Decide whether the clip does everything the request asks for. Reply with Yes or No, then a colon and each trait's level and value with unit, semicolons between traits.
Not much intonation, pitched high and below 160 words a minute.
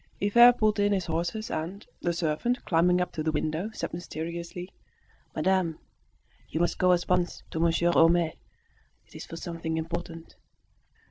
No: narrow, 2.2 semitones; medium, 170 Hz; average, 150 wpm